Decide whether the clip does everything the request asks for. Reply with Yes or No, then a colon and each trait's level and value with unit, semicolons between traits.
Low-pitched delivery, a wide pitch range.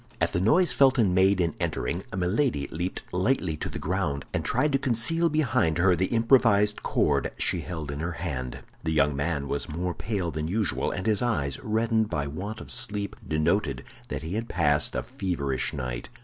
Yes: very low, 90 Hz; wide, 6.2 semitones